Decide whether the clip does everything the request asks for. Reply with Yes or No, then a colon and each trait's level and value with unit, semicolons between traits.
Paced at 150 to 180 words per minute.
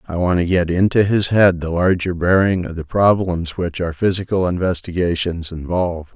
Yes: average, 175 wpm